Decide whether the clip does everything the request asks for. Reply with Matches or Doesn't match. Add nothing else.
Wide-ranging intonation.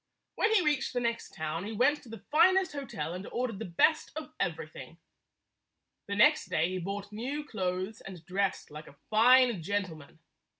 Matches